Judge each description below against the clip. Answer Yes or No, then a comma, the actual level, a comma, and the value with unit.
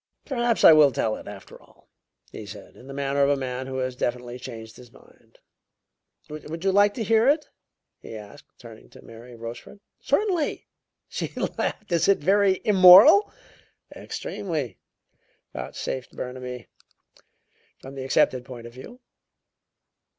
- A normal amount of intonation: No, wide, 7.9 semitones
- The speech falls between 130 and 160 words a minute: Yes, average, 145 wpm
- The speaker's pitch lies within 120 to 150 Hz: Yes, low, 135 Hz